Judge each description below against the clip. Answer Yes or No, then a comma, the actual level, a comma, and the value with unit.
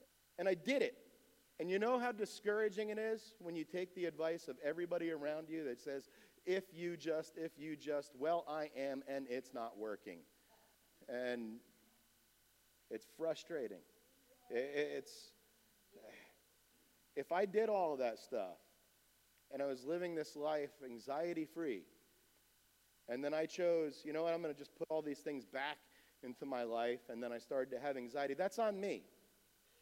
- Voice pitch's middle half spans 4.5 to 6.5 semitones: Yes, average, 5.2 semitones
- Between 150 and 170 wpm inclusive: Yes, average, 165 wpm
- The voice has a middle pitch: Yes, medium, 160 Hz